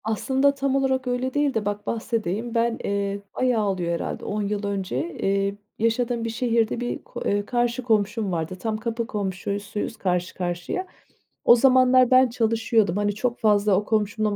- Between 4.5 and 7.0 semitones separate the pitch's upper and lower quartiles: No, average, 3.3 semitones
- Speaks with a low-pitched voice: No, high, 220 Hz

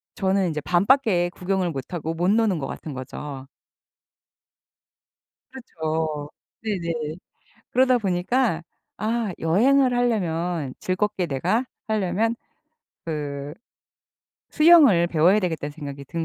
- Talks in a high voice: No, medium, 175 Hz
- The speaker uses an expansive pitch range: Yes, wide, 5.7 semitones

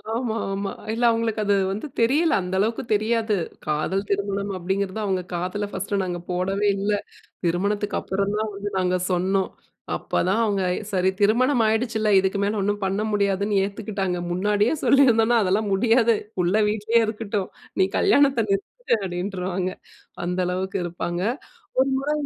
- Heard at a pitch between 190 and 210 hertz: Yes, high, 200 Hz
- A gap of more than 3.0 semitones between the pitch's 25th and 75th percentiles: No, average, 2.7 semitones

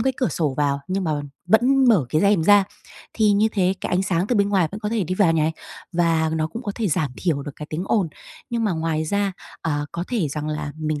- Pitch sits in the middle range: Yes, medium, 180 Hz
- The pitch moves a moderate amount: Yes, average, 4.7 semitones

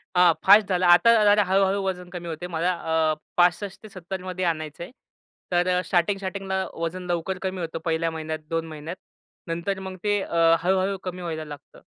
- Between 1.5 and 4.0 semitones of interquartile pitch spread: Yes, narrow, 2.4 semitones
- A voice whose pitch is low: No, medium, 180 Hz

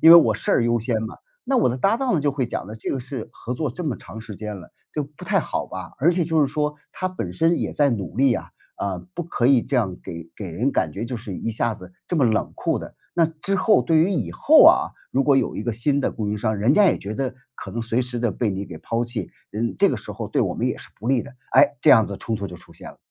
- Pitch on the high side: No, low, 120 Hz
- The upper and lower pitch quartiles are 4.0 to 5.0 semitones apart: No, wide, 5.6 semitones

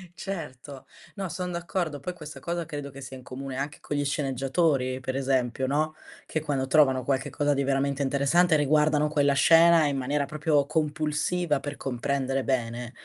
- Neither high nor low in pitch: Yes, medium, 145 Hz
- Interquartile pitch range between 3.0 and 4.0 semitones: No, narrow, 2.6 semitones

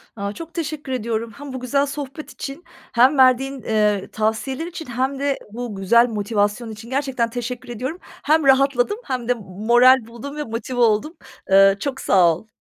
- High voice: Yes, high, 245 Hz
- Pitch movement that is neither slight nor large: Yes, average, 4.0 semitones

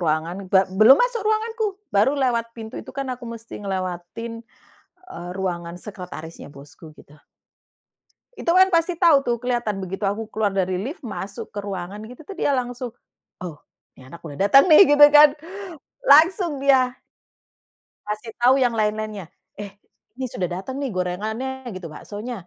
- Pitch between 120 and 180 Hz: No, high, 220 Hz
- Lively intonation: Yes, wide, 6.3 semitones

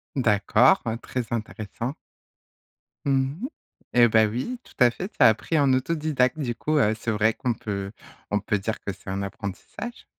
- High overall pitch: No, low, 120 Hz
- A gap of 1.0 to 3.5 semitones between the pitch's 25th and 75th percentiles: No, average, 4.2 semitones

